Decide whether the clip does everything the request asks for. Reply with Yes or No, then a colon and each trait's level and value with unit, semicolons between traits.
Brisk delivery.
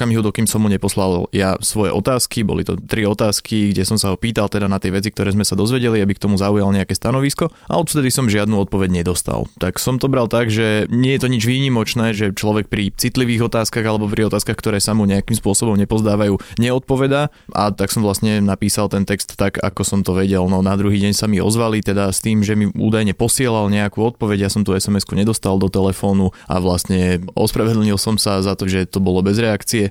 Yes: fast, 220 wpm